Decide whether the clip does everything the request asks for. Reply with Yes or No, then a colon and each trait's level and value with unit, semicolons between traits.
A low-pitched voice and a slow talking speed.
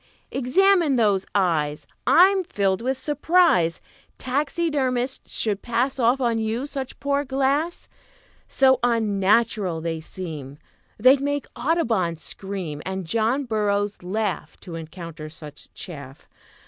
No: high, 225 Hz; slow, 115 wpm